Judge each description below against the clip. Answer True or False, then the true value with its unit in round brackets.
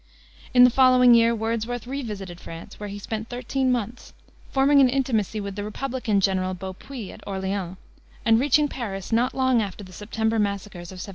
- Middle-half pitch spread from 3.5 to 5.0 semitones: True (4.1 semitones)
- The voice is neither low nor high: False (225 Hz)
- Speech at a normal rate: True (180 wpm)